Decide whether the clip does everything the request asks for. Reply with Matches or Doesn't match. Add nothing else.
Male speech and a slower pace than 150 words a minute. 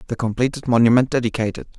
Matches